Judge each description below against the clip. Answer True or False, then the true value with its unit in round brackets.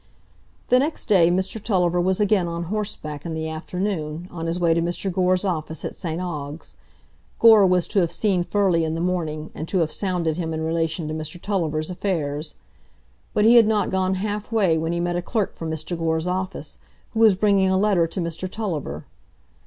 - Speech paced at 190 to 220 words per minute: True (200 wpm)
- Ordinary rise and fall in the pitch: True (3.3 semitones)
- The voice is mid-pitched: True (175 Hz)